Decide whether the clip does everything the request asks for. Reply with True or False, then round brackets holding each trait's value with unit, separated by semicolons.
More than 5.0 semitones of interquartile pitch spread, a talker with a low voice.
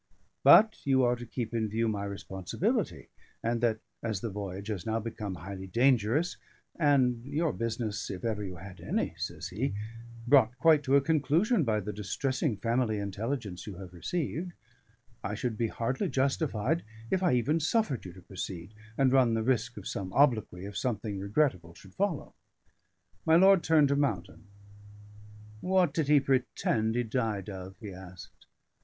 True (5.6 semitones; 115 Hz)